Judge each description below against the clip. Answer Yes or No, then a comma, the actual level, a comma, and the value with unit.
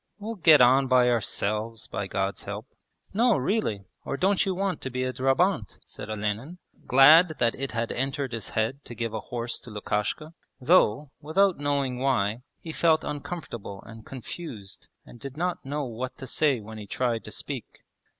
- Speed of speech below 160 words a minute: No, average, 180 wpm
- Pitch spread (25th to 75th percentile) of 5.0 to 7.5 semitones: Yes, wide, 5.5 semitones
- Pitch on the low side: Yes, low, 130 Hz